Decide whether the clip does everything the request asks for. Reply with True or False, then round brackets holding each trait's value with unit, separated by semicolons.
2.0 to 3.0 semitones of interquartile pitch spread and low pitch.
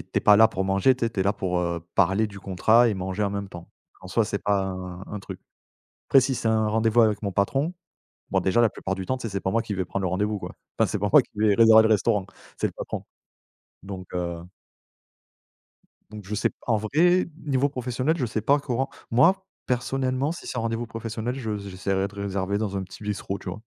False (3.5 semitones; 105 Hz)